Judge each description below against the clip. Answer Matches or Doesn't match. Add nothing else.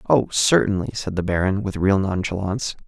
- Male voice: Matches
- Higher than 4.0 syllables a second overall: Matches